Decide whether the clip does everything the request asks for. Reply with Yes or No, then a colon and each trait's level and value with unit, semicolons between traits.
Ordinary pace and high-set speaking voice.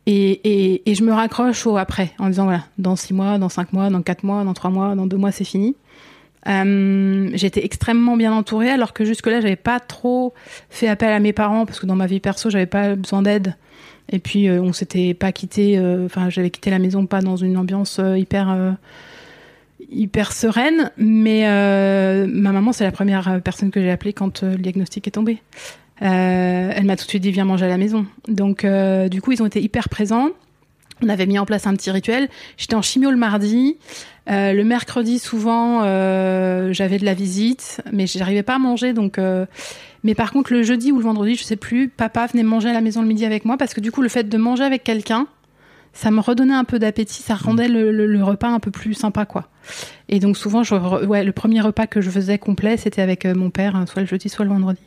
No: fast, 235 wpm; high, 205 Hz